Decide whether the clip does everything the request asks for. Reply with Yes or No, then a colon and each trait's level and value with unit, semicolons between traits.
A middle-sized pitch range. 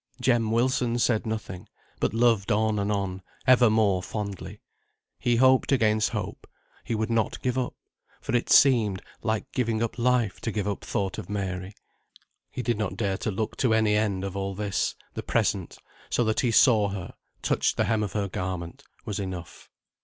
Yes: average, 3.0 semitones